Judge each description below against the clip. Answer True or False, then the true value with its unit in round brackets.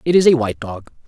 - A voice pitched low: True (130 Hz)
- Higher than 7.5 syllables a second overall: False (7.1 syllables/s)